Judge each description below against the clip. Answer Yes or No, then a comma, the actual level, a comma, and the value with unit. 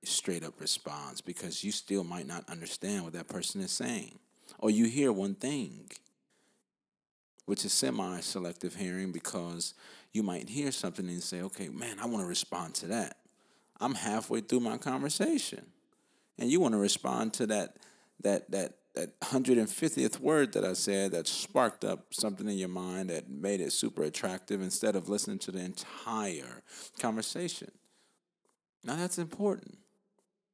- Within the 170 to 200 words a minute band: No, average, 155 wpm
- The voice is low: Yes, low, 105 Hz